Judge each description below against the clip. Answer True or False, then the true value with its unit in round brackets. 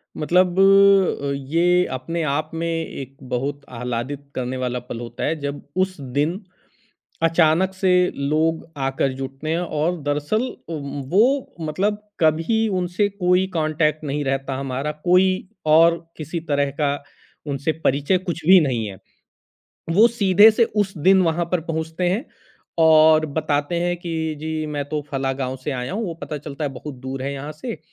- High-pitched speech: False (155 Hz)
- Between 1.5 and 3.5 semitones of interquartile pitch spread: False (4.0 semitones)